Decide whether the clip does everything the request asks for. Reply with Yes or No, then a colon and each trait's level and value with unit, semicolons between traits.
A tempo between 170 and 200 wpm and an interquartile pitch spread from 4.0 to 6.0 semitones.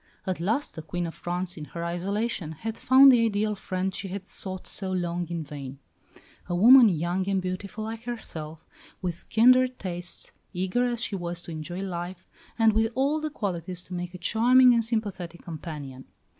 Yes: average, 185 wpm; average, 4.4 semitones